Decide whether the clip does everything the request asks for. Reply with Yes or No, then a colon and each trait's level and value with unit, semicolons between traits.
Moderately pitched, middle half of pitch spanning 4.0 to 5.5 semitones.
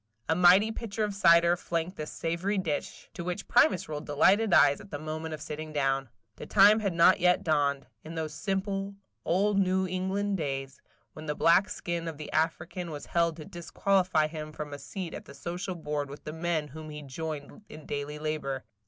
No: medium, 165 Hz; average, 3.6 semitones